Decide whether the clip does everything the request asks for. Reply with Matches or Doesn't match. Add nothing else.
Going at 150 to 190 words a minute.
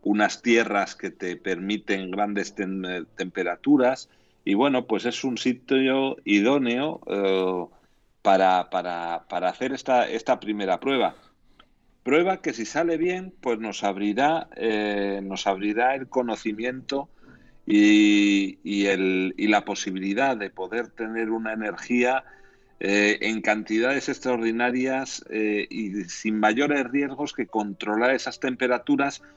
Doesn't match